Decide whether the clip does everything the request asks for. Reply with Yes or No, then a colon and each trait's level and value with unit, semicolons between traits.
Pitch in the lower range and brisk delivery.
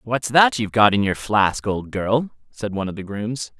Yes: low, 110 Hz; fast, 235 wpm